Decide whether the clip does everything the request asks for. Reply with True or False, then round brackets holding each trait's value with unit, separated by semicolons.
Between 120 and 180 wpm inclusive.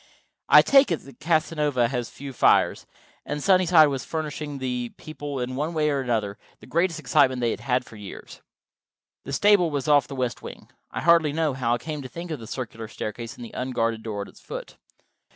False (205 wpm)